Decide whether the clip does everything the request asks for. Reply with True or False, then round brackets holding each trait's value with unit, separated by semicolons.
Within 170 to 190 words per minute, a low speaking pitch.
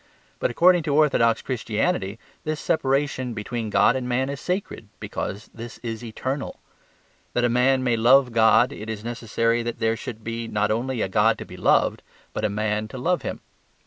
True (185 wpm; 120 Hz)